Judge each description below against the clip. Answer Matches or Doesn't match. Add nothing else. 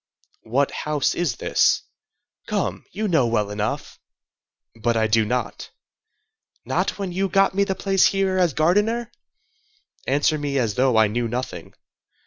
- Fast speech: Doesn't match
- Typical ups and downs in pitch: Doesn't match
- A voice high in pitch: Doesn't match